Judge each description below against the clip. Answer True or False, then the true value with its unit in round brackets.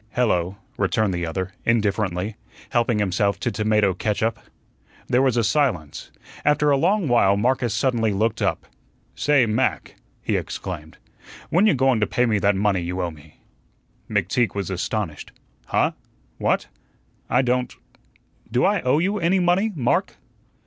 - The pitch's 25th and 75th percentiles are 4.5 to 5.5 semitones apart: True (5.0 semitones)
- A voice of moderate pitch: False (110 Hz)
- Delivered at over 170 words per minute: False (150 wpm)